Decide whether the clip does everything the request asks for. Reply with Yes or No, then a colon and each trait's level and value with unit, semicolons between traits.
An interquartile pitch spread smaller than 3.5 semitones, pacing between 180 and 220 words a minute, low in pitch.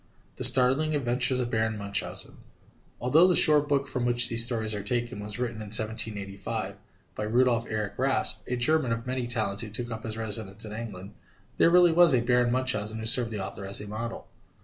Yes: average, 2.9 semitones; average, 200 wpm; low, 115 Hz